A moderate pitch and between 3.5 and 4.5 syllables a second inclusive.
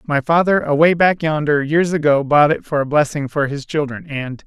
No: medium, 150 Hz; 5.1 syllables/s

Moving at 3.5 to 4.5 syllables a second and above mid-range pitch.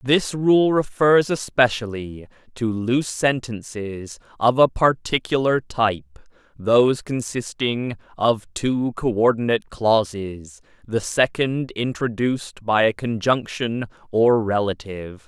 No: 4.0 syllables/s; low, 120 Hz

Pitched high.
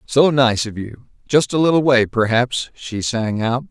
No: low, 125 Hz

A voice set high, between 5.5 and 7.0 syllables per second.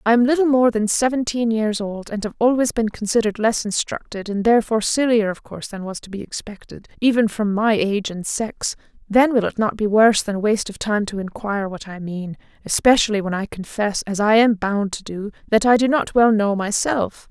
Yes: high, 215 Hz; 5.6 syllables/s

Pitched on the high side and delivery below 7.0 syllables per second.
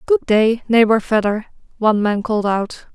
Yes: high, 220 Hz; 5.1 syllables/s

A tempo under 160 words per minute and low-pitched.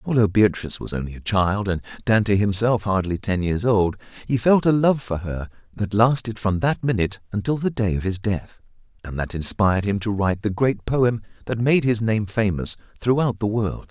No: fast, 205 wpm; low, 105 Hz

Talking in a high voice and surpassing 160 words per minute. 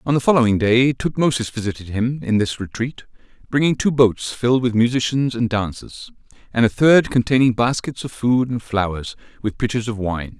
No: low, 120 Hz; average, 180 wpm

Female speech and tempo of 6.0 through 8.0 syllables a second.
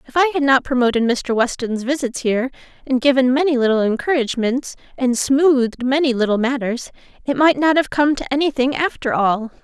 No: female; 5.7 syllables/s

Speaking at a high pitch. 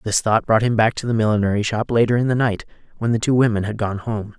No: low, 110 Hz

